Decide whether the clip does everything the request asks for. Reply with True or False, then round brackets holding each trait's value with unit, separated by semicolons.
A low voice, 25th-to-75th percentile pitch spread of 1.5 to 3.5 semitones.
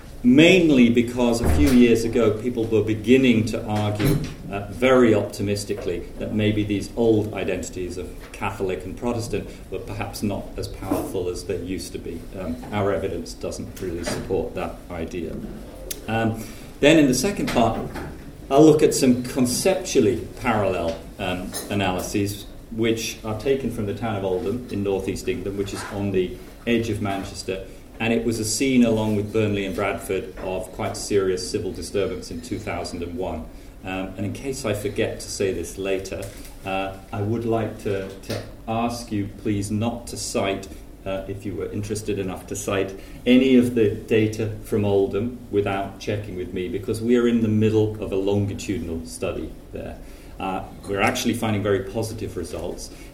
True (105 Hz; 2.9 semitones)